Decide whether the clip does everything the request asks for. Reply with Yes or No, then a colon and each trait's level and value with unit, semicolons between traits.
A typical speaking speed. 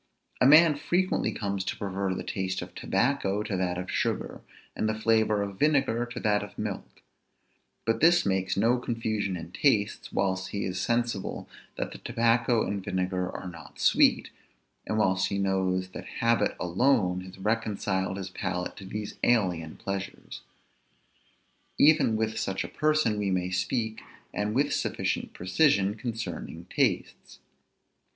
Yes: average, 150 wpm